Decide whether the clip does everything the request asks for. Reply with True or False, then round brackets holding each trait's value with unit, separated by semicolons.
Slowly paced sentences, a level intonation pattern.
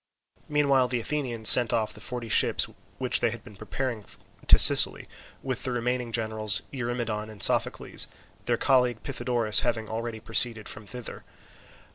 False (150 wpm; 2.2 semitones)